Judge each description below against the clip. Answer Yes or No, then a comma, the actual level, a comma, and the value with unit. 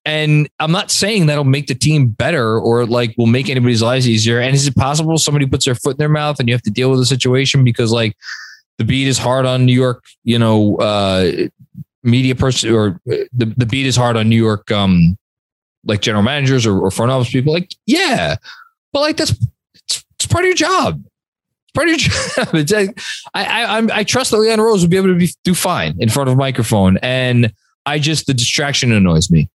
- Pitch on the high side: No, low, 130 Hz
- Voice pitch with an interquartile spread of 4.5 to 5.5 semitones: Yes, average, 4.9 semitones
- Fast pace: Yes, fast, 225 wpm